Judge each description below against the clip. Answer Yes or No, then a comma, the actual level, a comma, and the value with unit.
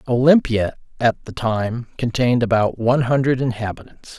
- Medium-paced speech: No, slow, 130 wpm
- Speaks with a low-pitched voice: Yes, low, 120 Hz